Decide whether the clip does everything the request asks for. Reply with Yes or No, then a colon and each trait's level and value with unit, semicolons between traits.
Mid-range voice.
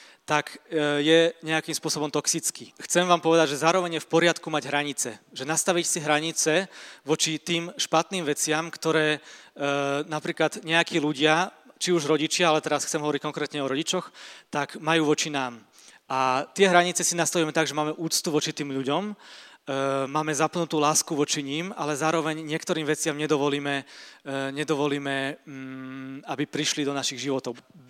Yes: medium, 155 Hz